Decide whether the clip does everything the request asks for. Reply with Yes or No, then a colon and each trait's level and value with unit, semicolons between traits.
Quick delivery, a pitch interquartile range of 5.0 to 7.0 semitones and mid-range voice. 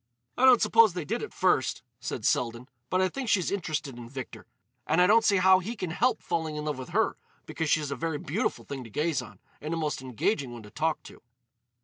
Yes: fast, 235 wpm; wide, 5.4 semitones; medium, 160 Hz